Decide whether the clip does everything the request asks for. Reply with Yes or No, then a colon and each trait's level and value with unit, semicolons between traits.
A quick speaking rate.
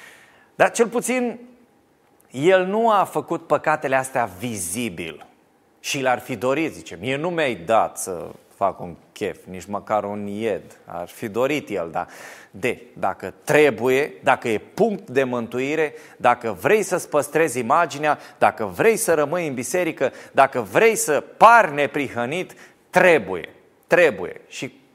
No: average, 140 wpm